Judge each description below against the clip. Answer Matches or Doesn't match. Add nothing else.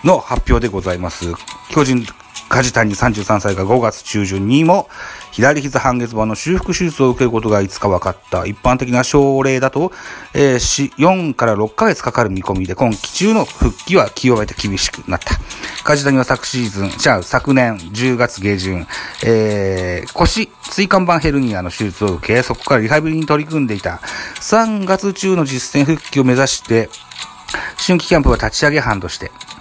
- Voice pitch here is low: Matches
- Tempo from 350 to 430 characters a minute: Doesn't match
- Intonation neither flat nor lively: Doesn't match